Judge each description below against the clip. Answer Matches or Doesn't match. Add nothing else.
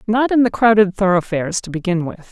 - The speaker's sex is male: Doesn't match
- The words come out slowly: Doesn't match